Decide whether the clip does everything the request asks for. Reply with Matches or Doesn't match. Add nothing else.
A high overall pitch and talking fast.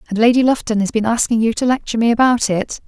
Matches